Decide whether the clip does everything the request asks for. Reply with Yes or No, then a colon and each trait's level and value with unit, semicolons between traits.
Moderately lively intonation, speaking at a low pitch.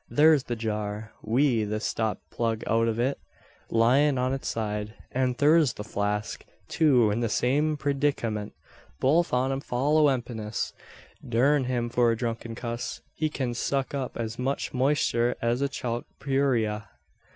Yes: average, 3.5 semitones; low, 120 Hz